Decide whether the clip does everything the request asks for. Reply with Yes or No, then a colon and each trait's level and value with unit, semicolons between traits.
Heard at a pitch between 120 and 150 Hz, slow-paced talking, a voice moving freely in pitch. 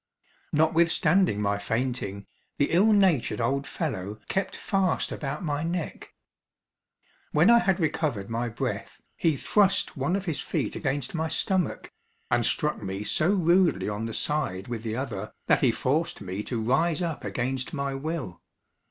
No: medium, 140 Hz; average, 155 wpm; wide, 6.8 semitones